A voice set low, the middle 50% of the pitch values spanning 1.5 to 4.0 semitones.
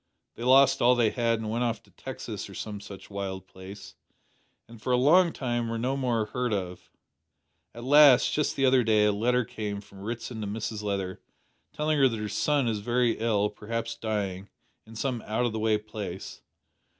Yes: low, 115 Hz; average, 3.1 semitones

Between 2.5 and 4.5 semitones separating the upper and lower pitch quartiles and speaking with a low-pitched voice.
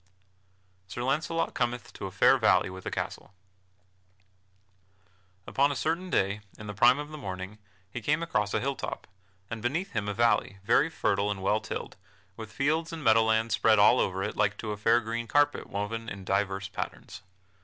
No: average, 5.2 semitones; low, 110 Hz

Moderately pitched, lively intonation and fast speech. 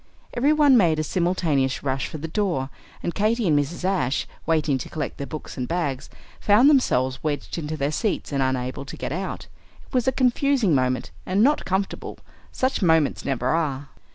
No: medium, 160 Hz; wide, 6.8 semitones; average, 185 wpm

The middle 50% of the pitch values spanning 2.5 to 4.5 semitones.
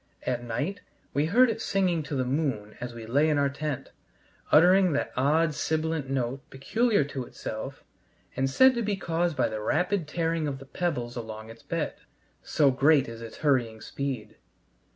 No: average, 4.9 semitones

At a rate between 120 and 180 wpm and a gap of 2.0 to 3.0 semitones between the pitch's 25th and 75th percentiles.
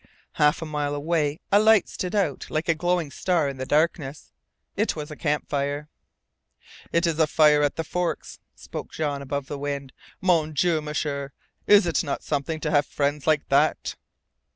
Yes: average, 175 wpm; narrow, 2.6 semitones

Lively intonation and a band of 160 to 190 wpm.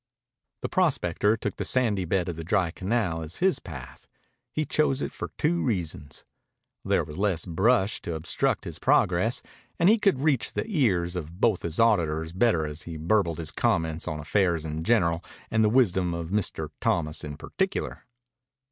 Yes: wide, 6.1 semitones; average, 175 wpm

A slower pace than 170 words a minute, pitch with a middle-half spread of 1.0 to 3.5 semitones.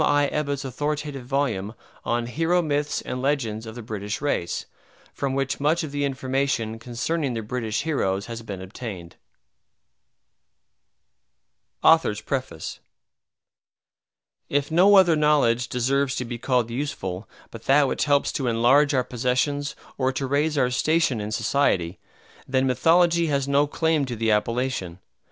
No: average, 140 wpm; average, 3.9 semitones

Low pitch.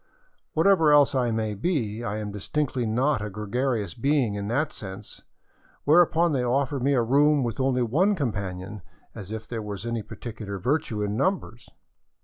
Yes: low, 120 Hz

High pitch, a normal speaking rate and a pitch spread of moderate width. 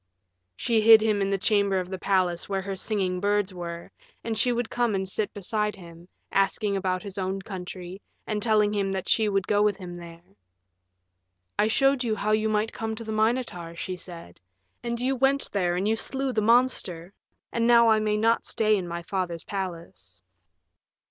Yes: high, 200 Hz; average, 195 wpm; average, 3.2 semitones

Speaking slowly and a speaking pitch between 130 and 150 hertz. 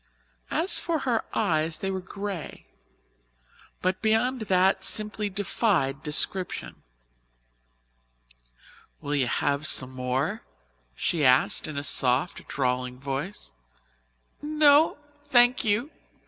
No: slow, 105 wpm; medium, 185 Hz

